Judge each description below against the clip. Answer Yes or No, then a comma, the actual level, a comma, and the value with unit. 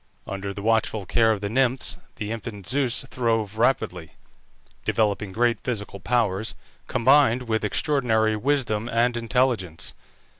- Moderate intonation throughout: Yes, average, 3.0 semitones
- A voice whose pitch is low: Yes, low, 115 Hz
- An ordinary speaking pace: No, slow, 125 wpm